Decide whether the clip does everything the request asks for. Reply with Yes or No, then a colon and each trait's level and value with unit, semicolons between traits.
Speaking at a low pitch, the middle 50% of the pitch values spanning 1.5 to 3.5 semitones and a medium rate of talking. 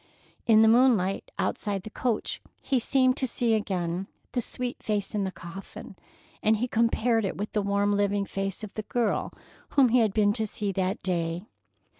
No: high, 210 Hz; average, 2.9 semitones; average, 185 wpm